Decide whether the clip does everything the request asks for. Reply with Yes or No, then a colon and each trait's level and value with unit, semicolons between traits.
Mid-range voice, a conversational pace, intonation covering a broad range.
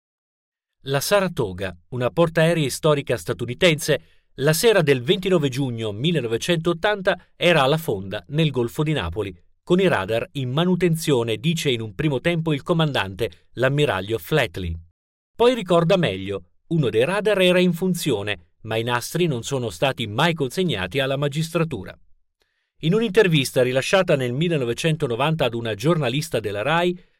Yes: medium, 145 Hz; average, 135 wpm; wide, 6.7 semitones